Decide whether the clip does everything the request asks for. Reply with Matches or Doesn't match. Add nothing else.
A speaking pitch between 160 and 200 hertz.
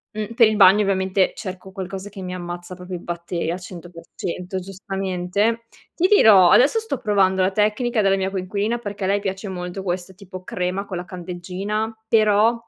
Matches